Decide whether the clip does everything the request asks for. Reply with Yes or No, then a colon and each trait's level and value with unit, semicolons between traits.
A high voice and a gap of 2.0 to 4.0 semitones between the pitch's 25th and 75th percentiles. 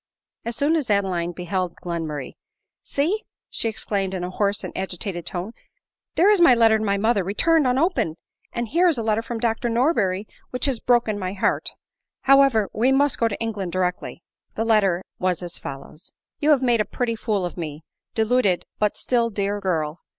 No: high, 215 Hz; average, 4.9 semitones